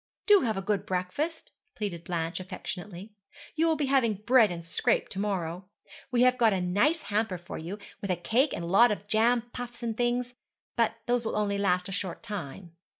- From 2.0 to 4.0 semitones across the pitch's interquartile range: No, average, 4.9 semitones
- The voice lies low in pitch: No, high, 210 Hz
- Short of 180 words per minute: No, fast, 205 wpm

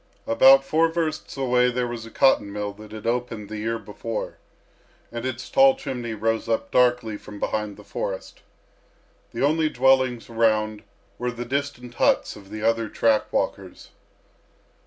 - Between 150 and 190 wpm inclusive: Yes, average, 155 wpm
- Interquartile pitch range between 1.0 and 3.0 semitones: No, average, 3.4 semitones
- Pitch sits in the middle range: No, low, 120 Hz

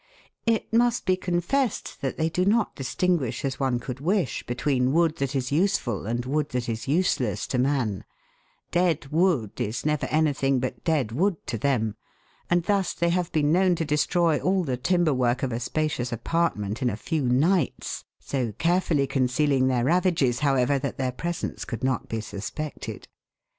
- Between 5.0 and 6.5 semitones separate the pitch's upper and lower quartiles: Yes, wide, 5.4 semitones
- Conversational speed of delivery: Yes, average, 180 wpm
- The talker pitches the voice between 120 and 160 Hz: Yes, medium, 140 Hz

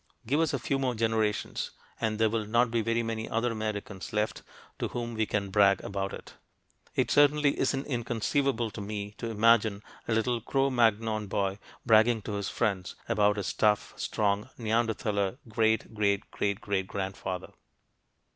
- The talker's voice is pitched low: Yes, low, 110 Hz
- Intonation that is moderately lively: No, narrow, 2.3 semitones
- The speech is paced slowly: No, average, 165 wpm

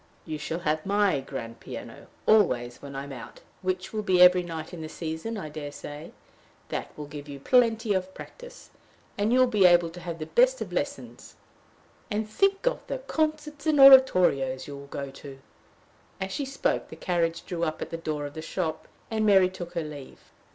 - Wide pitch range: Yes, wide, 6.3 semitones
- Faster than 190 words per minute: Yes, average, 200 wpm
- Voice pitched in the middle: Yes, medium, 175 Hz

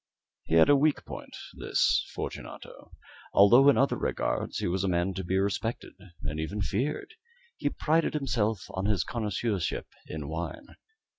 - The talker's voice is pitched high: No, low, 100 Hz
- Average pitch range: No, wide, 7.1 semitones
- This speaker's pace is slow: No, average, 155 wpm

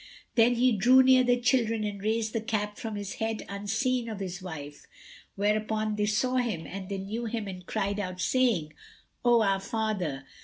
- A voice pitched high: Yes, high, 215 Hz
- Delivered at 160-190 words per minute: Yes, average, 185 wpm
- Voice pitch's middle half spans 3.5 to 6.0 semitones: No, average, 3.0 semitones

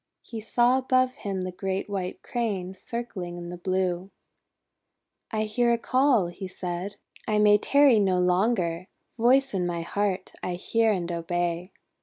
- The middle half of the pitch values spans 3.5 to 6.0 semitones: Yes, average, 4.4 semitones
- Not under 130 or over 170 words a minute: Yes, average, 160 wpm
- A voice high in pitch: Yes, high, 195 Hz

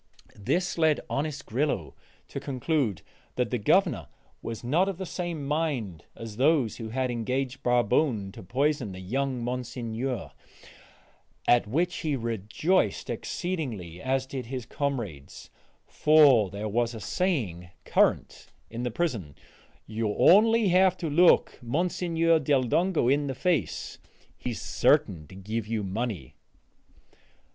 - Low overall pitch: Yes, low, 130 Hz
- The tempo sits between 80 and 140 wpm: Yes, slow, 135 wpm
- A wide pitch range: Yes, wide, 6.0 semitones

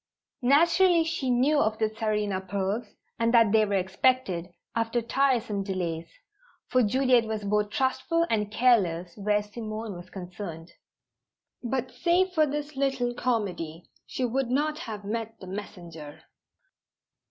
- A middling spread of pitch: Yes, average, 4.6 semitones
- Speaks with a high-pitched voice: Yes, high, 220 Hz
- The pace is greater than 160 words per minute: No, slow, 135 wpm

